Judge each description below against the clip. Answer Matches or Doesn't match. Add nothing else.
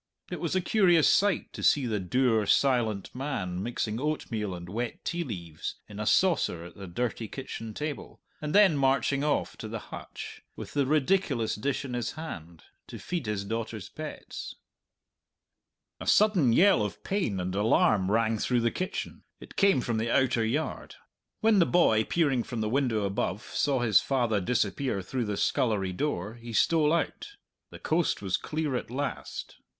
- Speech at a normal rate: Matches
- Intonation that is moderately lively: Doesn't match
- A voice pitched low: Matches